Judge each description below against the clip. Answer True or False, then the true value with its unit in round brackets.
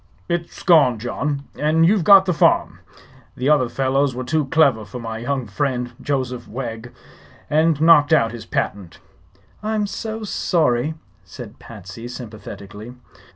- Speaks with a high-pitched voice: False (135 Hz)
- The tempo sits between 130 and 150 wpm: True (140 wpm)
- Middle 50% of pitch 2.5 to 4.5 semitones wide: False (5.1 semitones)